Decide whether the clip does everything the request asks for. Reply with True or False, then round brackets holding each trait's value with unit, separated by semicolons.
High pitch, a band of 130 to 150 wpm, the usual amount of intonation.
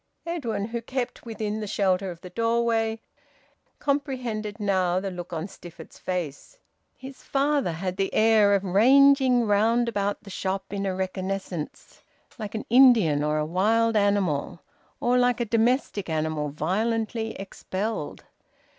True (205 Hz; 140 wpm; 4.0 semitones)